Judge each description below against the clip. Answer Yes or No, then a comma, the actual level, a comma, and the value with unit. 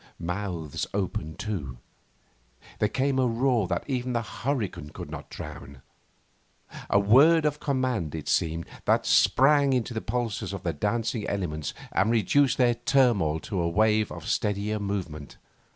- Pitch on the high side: No, low, 105 Hz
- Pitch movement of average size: No, wide, 6.3 semitones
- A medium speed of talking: Yes, average, 150 wpm